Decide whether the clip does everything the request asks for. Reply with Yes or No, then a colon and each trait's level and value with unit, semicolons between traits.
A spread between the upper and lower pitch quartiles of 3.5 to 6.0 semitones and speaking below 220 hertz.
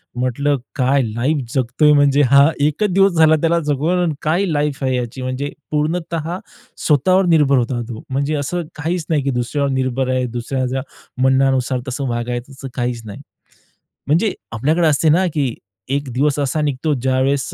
No: average, 3.1 semitones; medium, 140 Hz